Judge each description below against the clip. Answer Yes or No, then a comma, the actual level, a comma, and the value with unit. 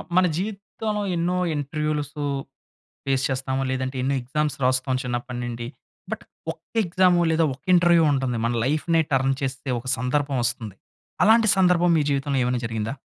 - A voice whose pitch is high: No, medium, 140 Hz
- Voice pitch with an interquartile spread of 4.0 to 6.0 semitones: Yes, average, 4.7 semitones